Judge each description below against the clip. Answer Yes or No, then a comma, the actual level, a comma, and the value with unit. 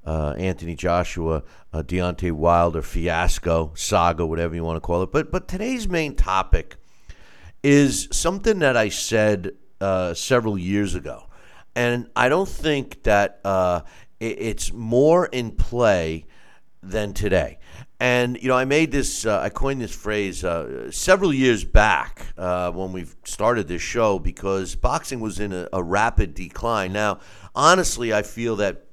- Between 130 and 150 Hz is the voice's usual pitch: No, very low, 95 Hz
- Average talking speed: Yes, average, 155 wpm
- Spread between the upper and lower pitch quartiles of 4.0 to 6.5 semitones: Yes, wide, 5.6 semitones